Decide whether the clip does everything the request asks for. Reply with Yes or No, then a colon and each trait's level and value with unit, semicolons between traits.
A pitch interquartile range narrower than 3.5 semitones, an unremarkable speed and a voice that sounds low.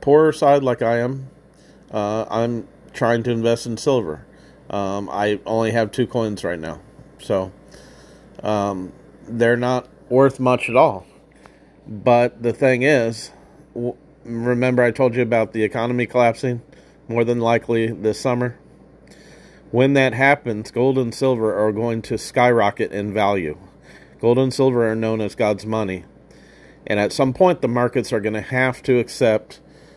Yes: narrow, 2.5 semitones; average, 155 wpm; low, 120 Hz